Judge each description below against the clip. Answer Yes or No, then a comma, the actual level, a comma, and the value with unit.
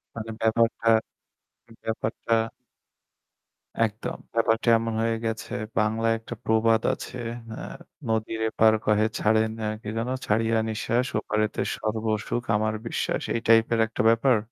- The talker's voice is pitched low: Yes, low, 110 Hz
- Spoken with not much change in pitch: Yes, narrow, 0.8 semitones